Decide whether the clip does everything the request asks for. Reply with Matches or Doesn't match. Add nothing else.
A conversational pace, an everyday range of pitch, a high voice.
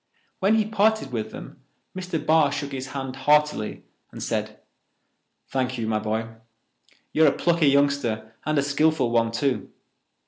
Doesn't match